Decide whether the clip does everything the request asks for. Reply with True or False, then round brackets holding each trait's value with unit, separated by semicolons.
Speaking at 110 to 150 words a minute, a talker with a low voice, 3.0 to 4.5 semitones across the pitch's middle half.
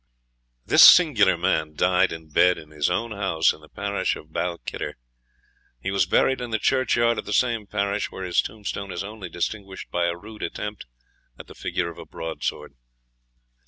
False (180 wpm; 95 Hz; 3.8 semitones)